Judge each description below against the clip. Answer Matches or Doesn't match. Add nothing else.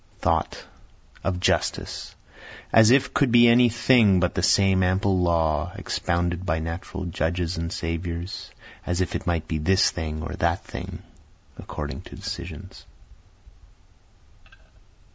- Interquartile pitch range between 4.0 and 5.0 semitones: Doesn't match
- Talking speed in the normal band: Doesn't match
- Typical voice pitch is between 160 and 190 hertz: Doesn't match